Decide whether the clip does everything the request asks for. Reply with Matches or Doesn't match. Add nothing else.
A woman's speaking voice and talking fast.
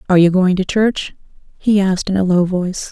Matches